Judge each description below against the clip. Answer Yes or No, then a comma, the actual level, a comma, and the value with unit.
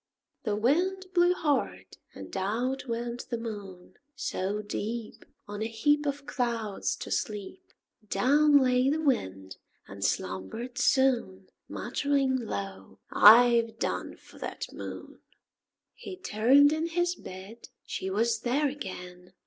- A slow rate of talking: Yes, slow, 125 wpm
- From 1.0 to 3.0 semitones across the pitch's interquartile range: No, wide, 5.5 semitones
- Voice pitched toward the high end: Yes, high, 240 Hz